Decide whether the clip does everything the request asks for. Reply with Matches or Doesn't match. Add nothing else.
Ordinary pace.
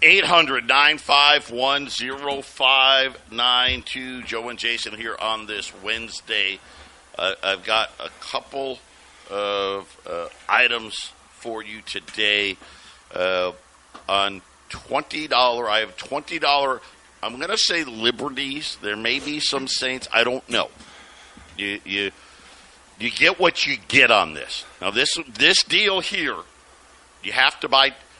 Doesn't match